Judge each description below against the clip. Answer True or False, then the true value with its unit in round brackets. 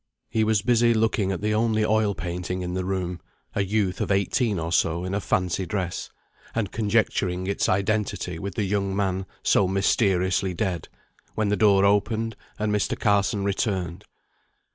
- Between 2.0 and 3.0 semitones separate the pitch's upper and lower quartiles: True (2.6 semitones)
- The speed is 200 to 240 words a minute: False (165 wpm)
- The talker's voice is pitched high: False (100 Hz)